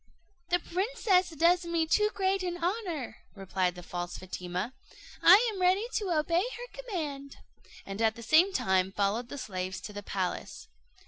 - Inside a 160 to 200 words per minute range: Yes, average, 165 wpm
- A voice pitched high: Yes, very high, 315 Hz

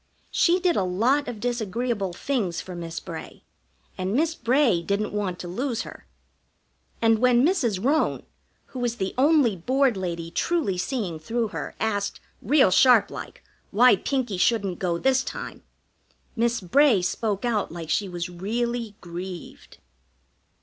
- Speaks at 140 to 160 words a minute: Yes, average, 145 wpm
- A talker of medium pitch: No, high, 220 Hz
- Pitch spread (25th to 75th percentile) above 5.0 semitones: Yes, wide, 5.5 semitones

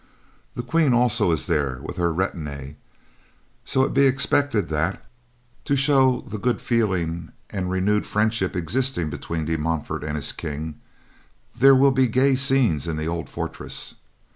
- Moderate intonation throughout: No, wide, 8.4 semitones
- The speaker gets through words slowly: No, average, 155 wpm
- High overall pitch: No, very low, 95 Hz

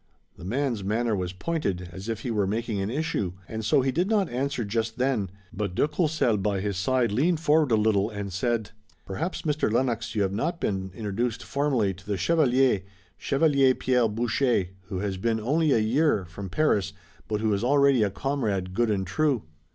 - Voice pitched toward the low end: Yes, low, 115 Hz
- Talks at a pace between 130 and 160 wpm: No, average, 200 wpm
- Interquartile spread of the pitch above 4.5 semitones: Yes, wide, 5.4 semitones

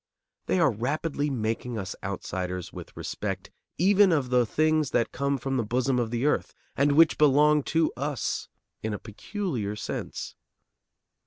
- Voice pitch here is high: No, low, 135 Hz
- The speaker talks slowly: No, average, 155 wpm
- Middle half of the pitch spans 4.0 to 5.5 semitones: Yes, average, 5.1 semitones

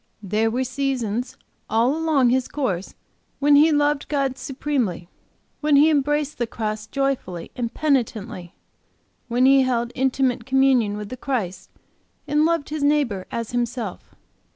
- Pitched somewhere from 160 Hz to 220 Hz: No, very high, 255 Hz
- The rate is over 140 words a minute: No, slow, 135 wpm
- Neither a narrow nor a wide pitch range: Yes, average, 4.2 semitones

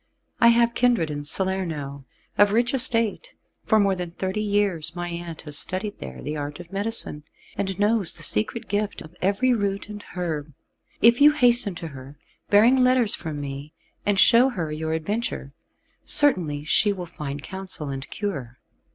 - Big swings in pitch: Yes, wide, 6.1 semitones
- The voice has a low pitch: No, high, 190 Hz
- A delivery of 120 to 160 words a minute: No, average, 170 wpm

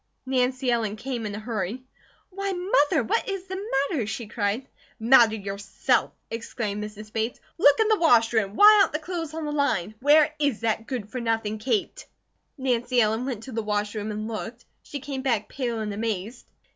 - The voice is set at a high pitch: Yes, high, 235 Hz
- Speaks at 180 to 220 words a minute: Yes, average, 190 wpm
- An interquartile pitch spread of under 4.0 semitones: No, average, 4.8 semitones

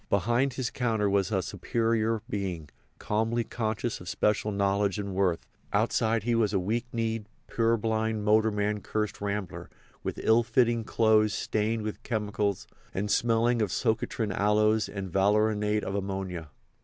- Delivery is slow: No, average, 145 wpm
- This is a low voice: Yes, low, 105 Hz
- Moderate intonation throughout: No, narrow, 2.0 semitones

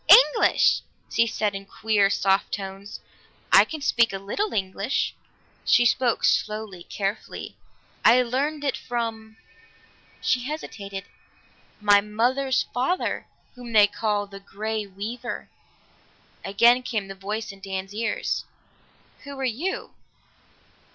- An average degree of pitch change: Yes, average, 3.8 semitones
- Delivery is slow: Yes, slow, 120 wpm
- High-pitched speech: Yes, high, 220 Hz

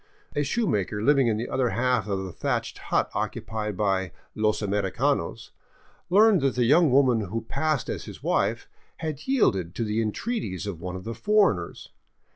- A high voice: No, low, 115 Hz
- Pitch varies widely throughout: Yes, wide, 6.3 semitones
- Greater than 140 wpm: Yes, average, 180 wpm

